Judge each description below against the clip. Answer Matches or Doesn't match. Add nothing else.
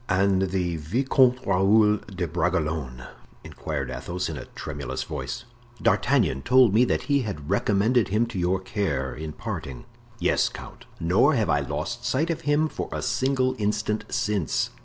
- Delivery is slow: Doesn't match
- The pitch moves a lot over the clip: Matches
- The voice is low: Matches